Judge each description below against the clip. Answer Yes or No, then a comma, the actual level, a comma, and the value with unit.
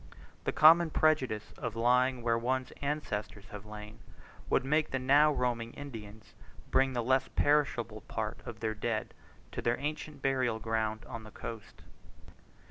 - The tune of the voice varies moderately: Yes, average, 3.7 semitones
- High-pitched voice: No, low, 120 Hz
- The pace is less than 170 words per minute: Yes, average, 150 wpm